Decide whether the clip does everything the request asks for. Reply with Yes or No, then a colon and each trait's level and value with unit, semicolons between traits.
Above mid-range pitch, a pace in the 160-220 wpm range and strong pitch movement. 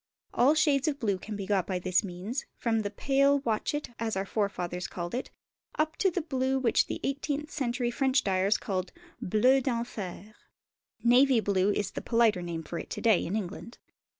Yes: high, 225 Hz; average, 185 wpm; wide, 5.7 semitones